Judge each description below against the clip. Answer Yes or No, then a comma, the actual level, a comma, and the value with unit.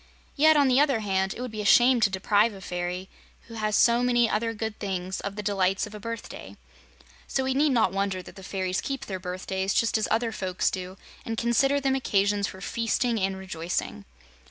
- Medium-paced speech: No, fast, 210 wpm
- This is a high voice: Yes, high, 210 Hz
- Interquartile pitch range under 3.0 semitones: No, average, 3.7 semitones